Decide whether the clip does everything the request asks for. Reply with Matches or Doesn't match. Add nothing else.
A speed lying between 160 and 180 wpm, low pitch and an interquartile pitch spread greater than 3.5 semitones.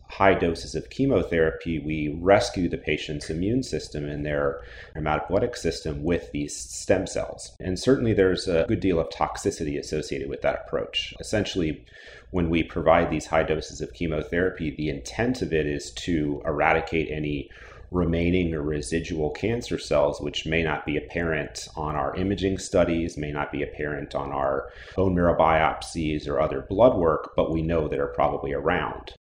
Doesn't match